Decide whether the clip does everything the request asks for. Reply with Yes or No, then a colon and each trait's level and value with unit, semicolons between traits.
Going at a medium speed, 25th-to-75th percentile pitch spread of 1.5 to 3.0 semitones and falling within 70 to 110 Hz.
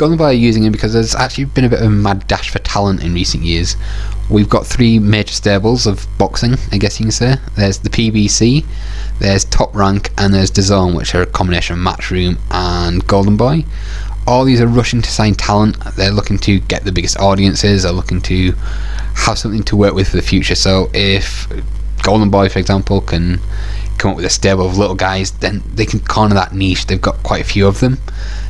No: fast, 215 wpm; narrow, 2.4 semitones; low, 100 Hz